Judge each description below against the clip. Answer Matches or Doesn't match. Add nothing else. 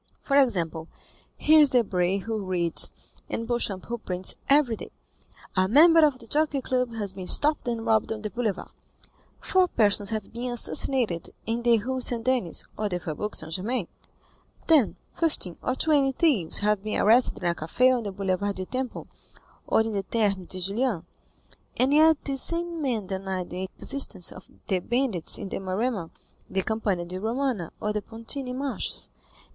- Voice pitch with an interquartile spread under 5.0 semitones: Doesn't match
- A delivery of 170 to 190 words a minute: Matches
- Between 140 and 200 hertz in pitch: Doesn't match